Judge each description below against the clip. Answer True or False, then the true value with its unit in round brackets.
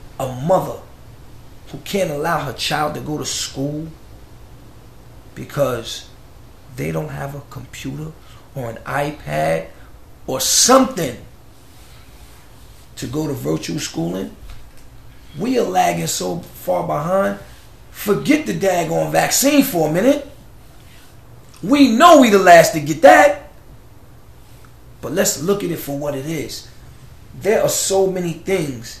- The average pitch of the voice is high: False (140 Hz)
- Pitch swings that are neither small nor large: False (7.4 semitones)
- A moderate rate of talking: False (130 wpm)